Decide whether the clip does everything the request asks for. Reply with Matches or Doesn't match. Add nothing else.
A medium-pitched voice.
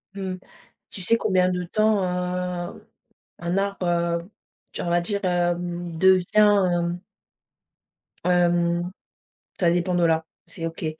Matches